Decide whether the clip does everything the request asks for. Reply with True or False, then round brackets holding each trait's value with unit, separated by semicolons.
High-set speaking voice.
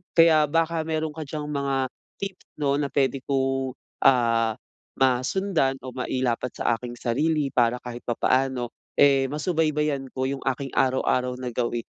False (135 Hz)